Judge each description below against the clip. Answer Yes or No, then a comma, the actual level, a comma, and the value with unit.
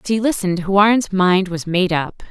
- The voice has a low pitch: No, high, 190 Hz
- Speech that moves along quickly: Yes, fast, 210 wpm